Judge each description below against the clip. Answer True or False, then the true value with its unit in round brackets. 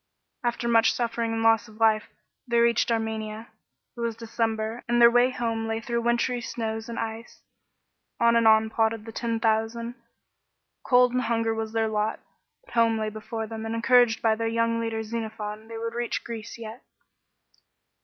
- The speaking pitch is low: False (225 Hz)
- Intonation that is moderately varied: False (1.0 semitones)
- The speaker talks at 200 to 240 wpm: False (175 wpm)